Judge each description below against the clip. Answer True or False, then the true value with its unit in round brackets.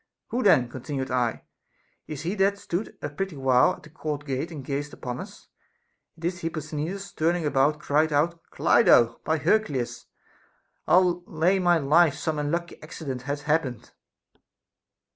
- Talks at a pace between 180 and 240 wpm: False (155 wpm)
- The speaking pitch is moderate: True (155 Hz)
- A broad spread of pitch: False (3.7 semitones)